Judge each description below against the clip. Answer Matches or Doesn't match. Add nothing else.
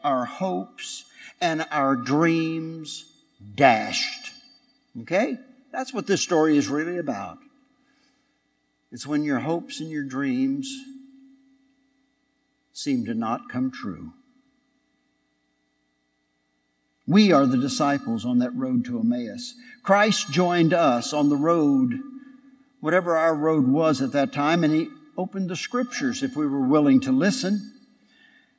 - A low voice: Doesn't match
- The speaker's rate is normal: Doesn't match